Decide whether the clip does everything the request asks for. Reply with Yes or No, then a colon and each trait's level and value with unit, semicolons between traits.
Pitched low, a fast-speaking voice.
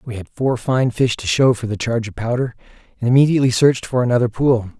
Yes: low, 120 Hz; fast, 225 wpm